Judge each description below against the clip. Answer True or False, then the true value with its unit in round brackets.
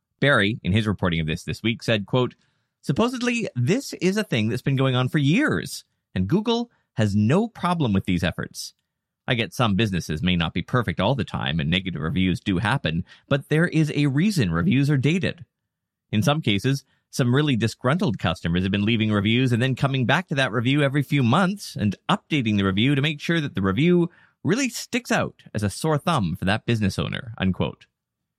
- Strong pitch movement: True (7.3 semitones)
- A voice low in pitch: True (130 Hz)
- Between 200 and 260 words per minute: True (205 wpm)